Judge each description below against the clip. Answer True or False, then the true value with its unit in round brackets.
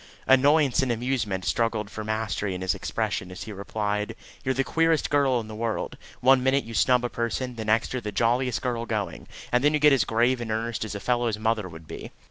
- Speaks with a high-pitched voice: False (115 Hz)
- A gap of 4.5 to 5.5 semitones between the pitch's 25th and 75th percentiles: False (3.2 semitones)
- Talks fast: True (230 wpm)